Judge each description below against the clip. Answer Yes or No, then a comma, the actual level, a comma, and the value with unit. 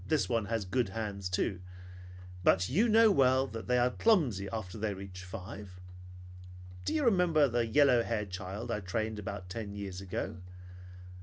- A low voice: Yes, low, 110 Hz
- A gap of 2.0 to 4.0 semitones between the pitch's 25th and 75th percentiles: No, average, 4.9 semitones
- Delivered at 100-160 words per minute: No, average, 170 wpm